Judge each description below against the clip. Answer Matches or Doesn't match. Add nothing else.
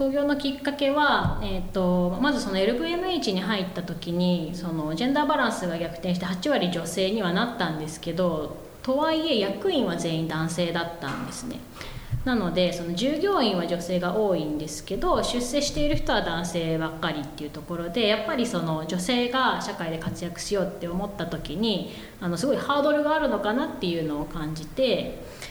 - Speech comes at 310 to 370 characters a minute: Doesn't match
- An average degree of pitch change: Doesn't match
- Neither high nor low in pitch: Matches